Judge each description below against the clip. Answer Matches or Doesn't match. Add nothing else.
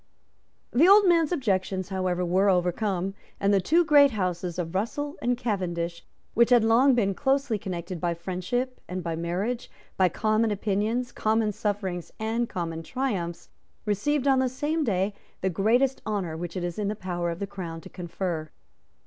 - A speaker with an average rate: Matches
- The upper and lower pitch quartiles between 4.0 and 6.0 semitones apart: Matches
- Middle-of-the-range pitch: Doesn't match